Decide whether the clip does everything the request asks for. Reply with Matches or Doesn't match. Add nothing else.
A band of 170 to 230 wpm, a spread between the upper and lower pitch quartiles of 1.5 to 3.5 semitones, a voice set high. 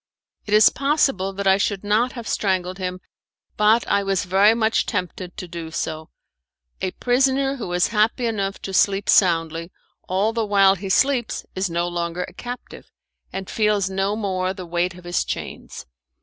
Matches